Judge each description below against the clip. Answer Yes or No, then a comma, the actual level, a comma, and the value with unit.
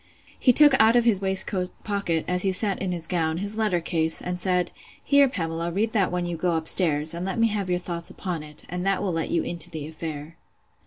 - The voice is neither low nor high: Yes, medium, 180 Hz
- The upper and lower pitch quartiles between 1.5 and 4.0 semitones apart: Yes, average, 3.3 semitones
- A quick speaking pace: Yes, fast, 240 wpm